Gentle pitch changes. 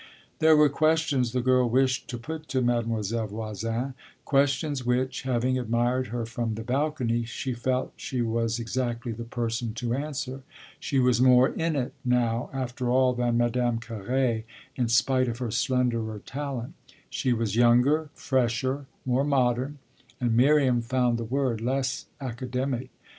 Yes: narrow, 2.1 semitones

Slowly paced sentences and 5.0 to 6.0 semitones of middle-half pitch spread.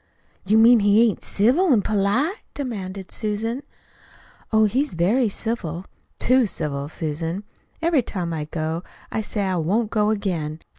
No: average, 145 wpm; average, 5.3 semitones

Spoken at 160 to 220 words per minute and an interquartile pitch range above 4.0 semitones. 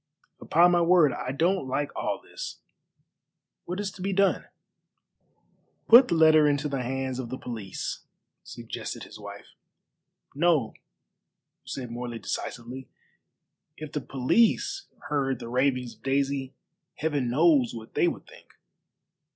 No: slow, 135 wpm; average, 4.9 semitones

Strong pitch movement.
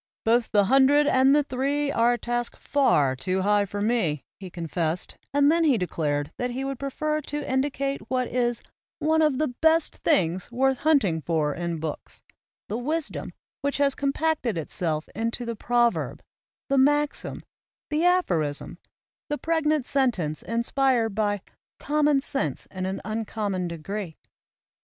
Yes: wide, 7.1 semitones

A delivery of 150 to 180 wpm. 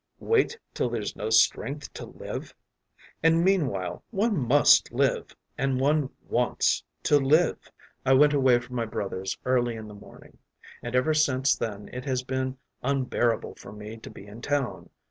Yes: average, 165 wpm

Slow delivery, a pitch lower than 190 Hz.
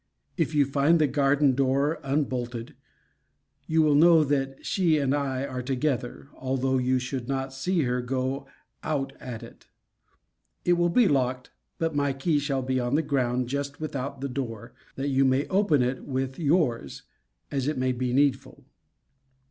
No: average, 165 wpm; low, 135 Hz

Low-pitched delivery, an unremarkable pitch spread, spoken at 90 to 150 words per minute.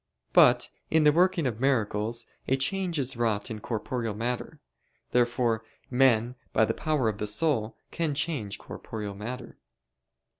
Yes: low, 120 Hz; average, 4.5 semitones; average, 145 wpm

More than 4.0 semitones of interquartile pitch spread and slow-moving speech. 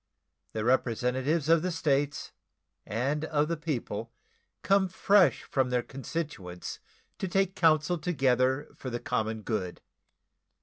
Yes: average, 5.1 semitones; slow, 125 wpm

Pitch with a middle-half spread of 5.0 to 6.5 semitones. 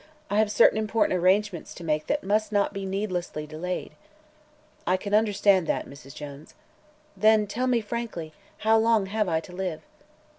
No: average, 3.6 semitones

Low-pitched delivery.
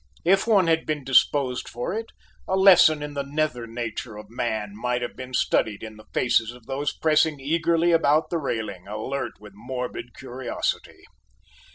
Yes: low, 130 Hz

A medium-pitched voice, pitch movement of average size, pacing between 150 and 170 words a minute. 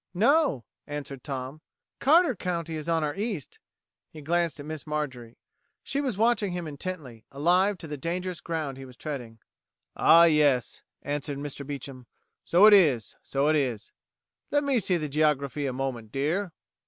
Yes: medium, 150 Hz; average, 4.6 semitones; average, 165 wpm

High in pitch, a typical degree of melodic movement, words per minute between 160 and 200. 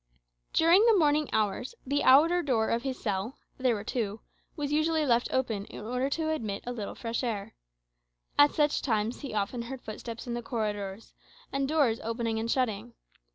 Yes: high, 240 Hz; average, 4.5 semitones; average, 180 wpm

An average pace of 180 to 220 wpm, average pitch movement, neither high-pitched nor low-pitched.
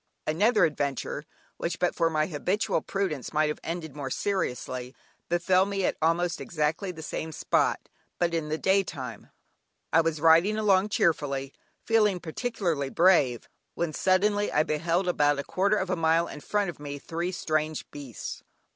No: average, 165 wpm; average, 3.8 semitones; medium, 165 Hz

